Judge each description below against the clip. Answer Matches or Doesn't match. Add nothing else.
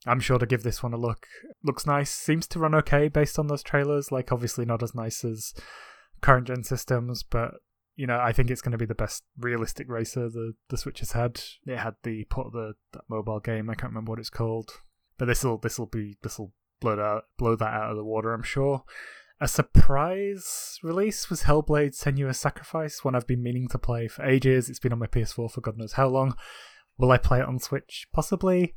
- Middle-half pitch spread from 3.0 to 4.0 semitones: Matches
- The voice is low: Matches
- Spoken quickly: Matches